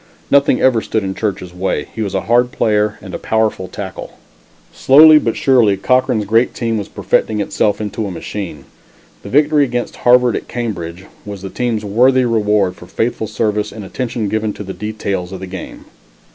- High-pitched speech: No, low, 110 Hz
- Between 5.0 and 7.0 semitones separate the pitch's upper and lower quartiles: No, average, 3.6 semitones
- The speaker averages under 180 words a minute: No, average, 185 wpm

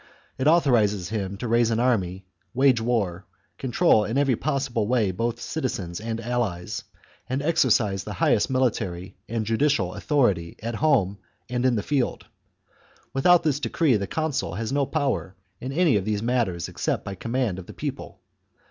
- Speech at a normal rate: Yes, average, 160 wpm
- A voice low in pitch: Yes, low, 115 Hz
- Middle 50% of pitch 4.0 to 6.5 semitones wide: Yes, average, 4.9 semitones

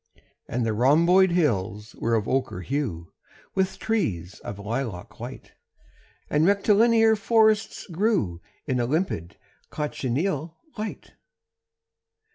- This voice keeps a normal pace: No, slow, 105 wpm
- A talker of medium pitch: Yes, medium, 150 Hz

